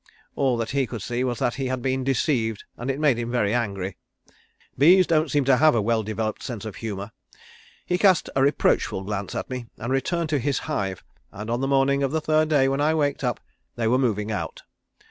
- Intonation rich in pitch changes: No, average, 4.0 semitones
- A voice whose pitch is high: No, low, 130 Hz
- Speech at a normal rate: No, fast, 220 wpm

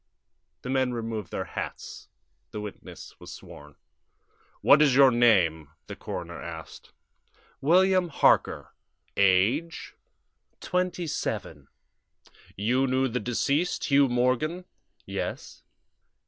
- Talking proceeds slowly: Yes, slow, 105 wpm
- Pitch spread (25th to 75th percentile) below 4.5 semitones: No, wide, 5.4 semitones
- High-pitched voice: No, low, 130 Hz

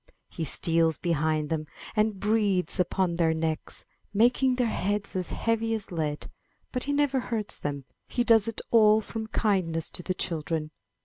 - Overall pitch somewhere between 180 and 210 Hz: Yes, high, 190 Hz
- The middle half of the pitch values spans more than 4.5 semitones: Yes, wide, 5.5 semitones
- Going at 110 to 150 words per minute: No, average, 165 wpm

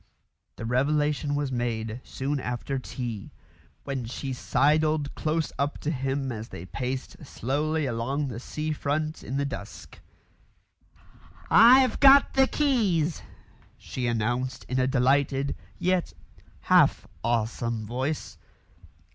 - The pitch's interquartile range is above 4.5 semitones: No, average, 3.8 semitones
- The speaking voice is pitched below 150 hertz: Yes, low, 135 Hz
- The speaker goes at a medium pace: No, slow, 120 wpm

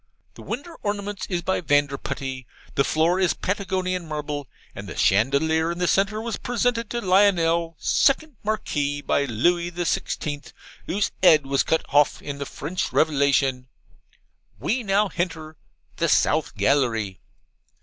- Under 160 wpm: Yes, average, 140 wpm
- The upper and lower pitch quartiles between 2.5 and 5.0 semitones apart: No, wide, 5.5 semitones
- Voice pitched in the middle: Yes, medium, 165 Hz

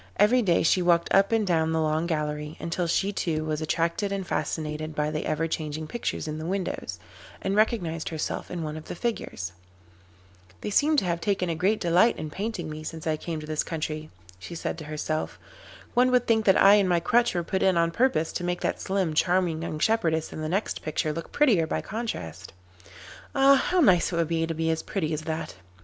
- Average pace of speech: No, fast, 220 wpm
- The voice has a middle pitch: Yes, medium, 165 Hz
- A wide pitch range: No, average, 4.0 semitones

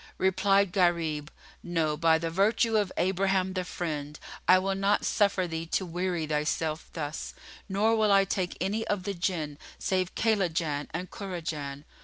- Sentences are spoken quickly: No, average, 155 wpm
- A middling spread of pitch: Yes, average, 3.3 semitones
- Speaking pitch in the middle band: Yes, medium, 180 Hz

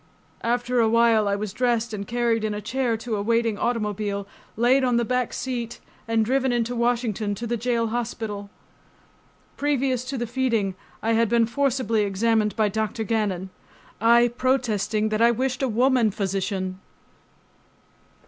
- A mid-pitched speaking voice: No, high, 230 Hz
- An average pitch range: No, narrow, 2.3 semitones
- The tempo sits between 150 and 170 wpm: Yes, average, 160 wpm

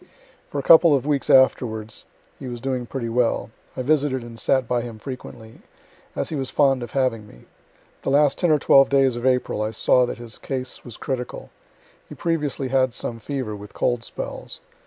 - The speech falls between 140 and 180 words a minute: No, average, 195 wpm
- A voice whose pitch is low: Yes, low, 130 Hz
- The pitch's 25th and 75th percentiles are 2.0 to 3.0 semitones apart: Yes, average, 2.7 semitones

